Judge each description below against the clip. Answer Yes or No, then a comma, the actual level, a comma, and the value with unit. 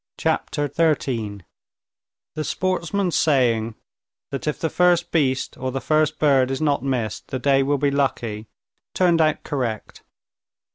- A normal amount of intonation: Yes, average, 3.5 semitones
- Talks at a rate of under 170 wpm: Yes, average, 140 wpm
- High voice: No, medium, 140 Hz